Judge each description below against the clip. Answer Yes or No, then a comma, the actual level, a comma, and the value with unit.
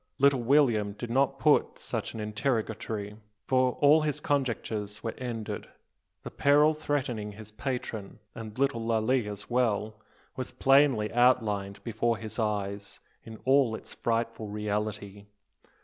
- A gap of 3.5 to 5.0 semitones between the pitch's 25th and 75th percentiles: Yes, average, 3.8 semitones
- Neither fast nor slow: No, slow, 130 wpm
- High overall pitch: No, low, 115 Hz